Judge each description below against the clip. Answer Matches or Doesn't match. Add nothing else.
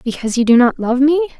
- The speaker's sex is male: Doesn't match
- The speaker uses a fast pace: Matches